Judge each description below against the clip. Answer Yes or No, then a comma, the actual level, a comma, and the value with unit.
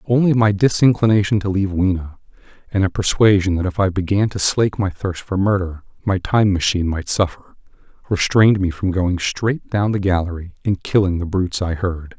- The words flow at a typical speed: Yes, average, 185 wpm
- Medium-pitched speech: No, very low, 95 Hz